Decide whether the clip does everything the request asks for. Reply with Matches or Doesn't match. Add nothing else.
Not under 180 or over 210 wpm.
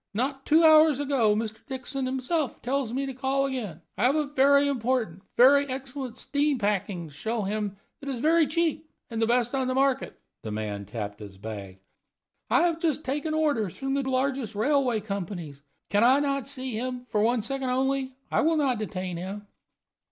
Matches